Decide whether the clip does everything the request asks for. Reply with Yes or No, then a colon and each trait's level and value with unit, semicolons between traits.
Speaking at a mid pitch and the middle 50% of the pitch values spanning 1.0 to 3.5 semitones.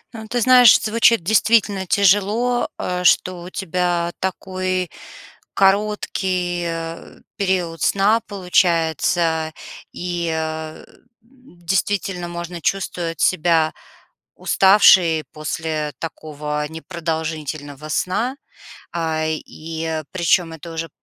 Yes: medium, 175 Hz; average, 3.1 semitones